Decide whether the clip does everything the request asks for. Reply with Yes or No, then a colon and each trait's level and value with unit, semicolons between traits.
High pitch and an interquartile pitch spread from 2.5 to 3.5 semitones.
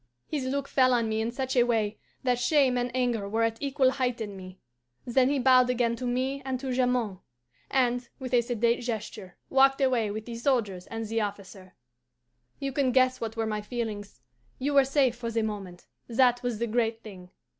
Yes: high, 240 Hz; average, 2.9 semitones